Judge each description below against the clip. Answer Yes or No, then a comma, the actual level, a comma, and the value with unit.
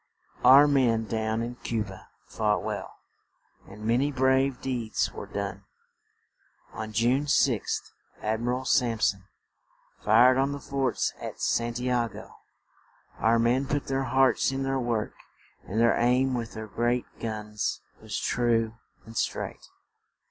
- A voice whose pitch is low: Yes, low, 120 Hz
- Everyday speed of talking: Yes, average, 150 wpm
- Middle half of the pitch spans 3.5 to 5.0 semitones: No, average, 2.9 semitones